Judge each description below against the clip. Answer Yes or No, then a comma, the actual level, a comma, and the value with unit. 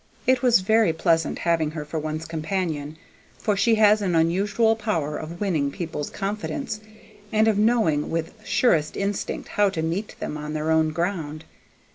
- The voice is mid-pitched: Yes, medium, 170 Hz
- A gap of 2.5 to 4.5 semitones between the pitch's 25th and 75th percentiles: No, average, 5.0 semitones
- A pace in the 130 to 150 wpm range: No, average, 165 wpm